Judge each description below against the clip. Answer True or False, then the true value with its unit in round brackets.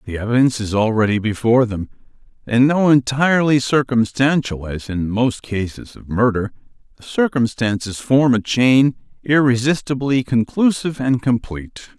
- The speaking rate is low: True (115 wpm)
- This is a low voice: True (125 Hz)